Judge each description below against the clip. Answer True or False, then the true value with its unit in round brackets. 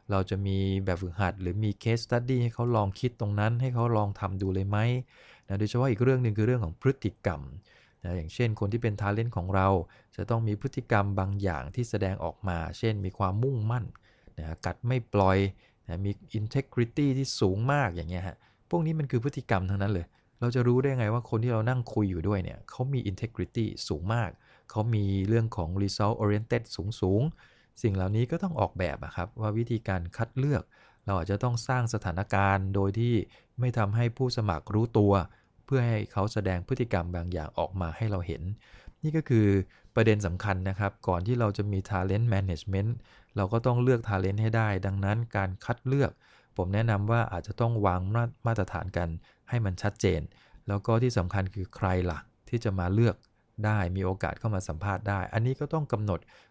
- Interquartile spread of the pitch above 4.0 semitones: False (3.7 semitones)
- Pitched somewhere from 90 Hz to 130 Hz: True (105 Hz)